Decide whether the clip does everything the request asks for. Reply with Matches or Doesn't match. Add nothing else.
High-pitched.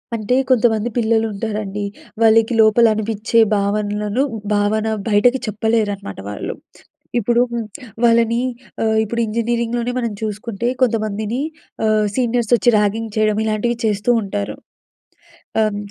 Matches